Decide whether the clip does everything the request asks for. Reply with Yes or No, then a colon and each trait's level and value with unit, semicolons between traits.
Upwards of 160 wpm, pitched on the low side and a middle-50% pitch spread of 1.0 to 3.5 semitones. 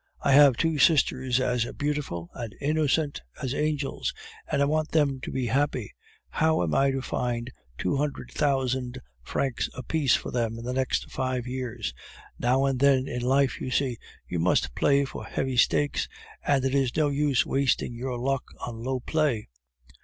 Yes: average, 175 wpm; low, 130 Hz; narrow, 2.4 semitones